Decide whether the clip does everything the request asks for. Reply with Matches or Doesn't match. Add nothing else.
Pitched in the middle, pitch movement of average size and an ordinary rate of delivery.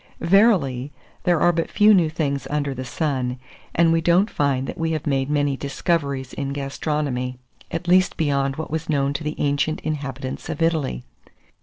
Matches